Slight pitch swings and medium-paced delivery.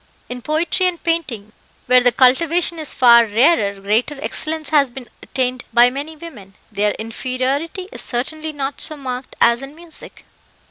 No: average, 4.7 semitones; average, 155 wpm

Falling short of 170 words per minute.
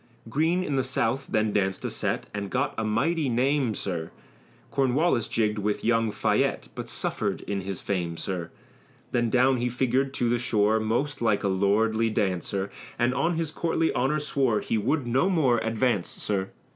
No: average, 175 wpm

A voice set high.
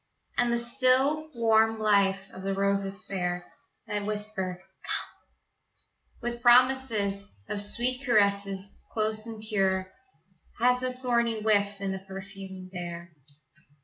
Yes: high, 205 Hz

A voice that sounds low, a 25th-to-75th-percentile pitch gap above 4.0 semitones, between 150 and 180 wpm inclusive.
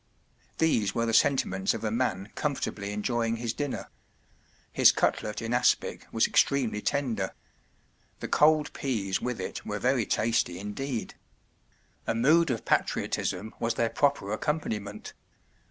No: low, 115 Hz; average, 4.4 semitones; average, 140 wpm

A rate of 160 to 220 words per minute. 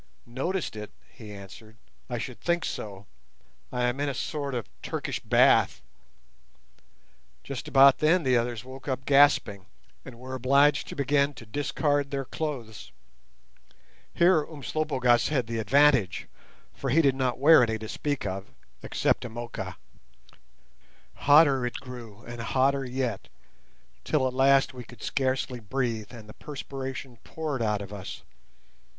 No: average, 145 wpm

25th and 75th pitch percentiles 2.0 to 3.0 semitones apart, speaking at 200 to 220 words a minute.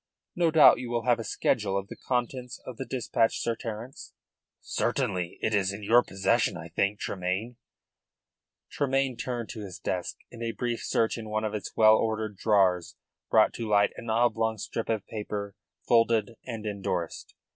No: average, 2.7 semitones; average, 175 wpm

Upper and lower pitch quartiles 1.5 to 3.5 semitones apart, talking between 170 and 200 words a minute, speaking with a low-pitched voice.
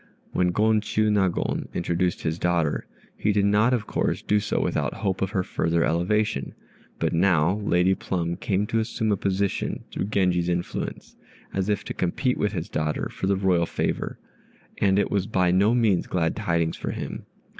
Yes: average, 3.1 semitones; average, 175 wpm; very low, 95 Hz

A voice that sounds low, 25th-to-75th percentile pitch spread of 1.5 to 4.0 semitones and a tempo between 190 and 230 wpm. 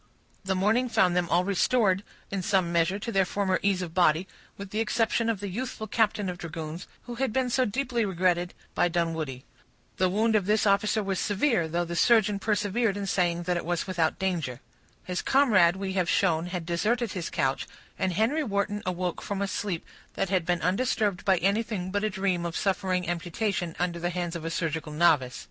No: high, 190 Hz; average, 3.2 semitones; average, 200 wpm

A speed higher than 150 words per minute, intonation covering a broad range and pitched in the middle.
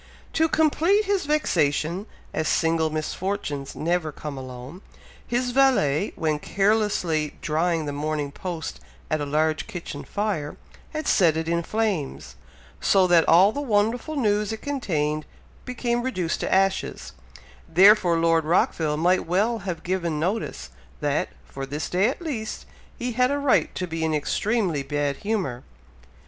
No: average, 145 wpm; wide, 6.2 semitones; medium, 175 Hz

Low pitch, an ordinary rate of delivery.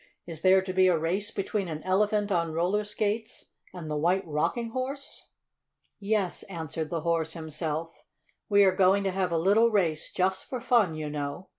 No: medium, 185 Hz; average, 180 wpm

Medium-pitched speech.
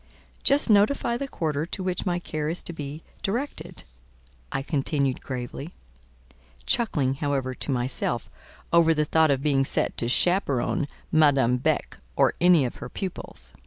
Yes: medium, 150 Hz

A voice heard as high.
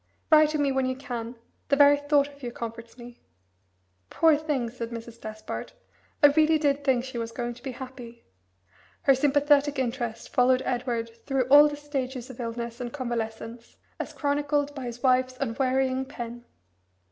Yes: very high, 255 Hz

